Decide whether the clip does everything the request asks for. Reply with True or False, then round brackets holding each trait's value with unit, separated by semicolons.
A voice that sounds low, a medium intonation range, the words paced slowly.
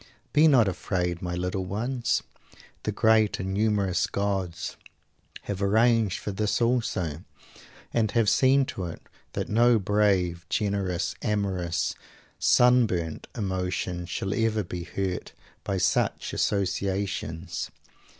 True (100 Hz; 3.4 semitones; 115 wpm)